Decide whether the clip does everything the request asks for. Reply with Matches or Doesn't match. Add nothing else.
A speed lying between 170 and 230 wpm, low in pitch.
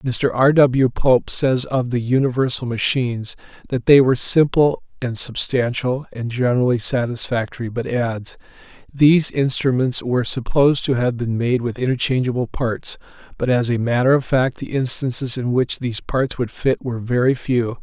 Doesn't match